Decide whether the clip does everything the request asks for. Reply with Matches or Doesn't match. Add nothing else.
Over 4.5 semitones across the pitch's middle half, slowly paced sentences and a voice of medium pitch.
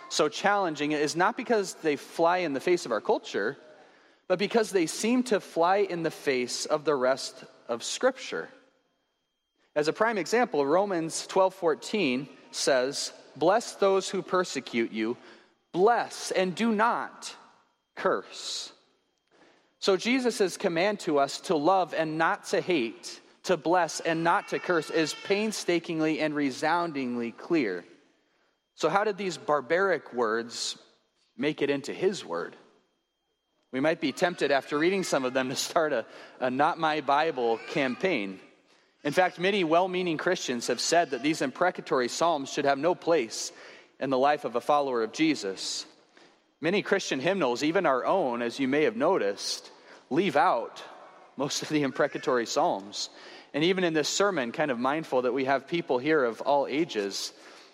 Doesn't match